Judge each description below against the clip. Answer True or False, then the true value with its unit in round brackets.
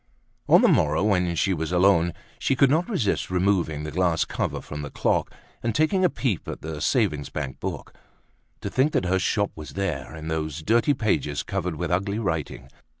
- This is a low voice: True (90 Hz)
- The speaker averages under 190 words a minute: False (195 wpm)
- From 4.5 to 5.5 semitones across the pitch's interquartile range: True (5.2 semitones)